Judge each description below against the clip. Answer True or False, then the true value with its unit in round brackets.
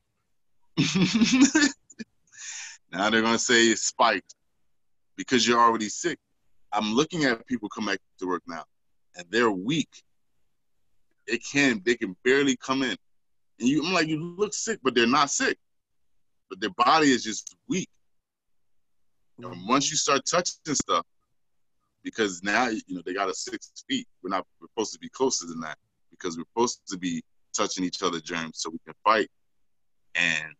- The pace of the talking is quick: False (165 wpm)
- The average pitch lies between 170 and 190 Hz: False (135 Hz)